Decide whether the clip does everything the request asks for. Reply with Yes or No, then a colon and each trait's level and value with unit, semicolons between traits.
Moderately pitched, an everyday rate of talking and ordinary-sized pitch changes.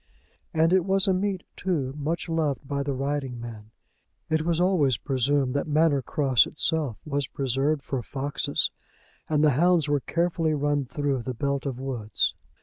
Yes: medium, 145 Hz; average, 165 wpm; average, 3.2 semitones